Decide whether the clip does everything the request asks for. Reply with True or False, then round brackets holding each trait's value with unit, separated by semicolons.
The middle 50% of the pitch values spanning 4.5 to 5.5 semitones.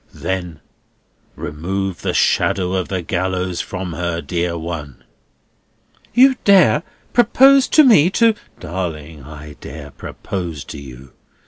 False (3.9 semitones)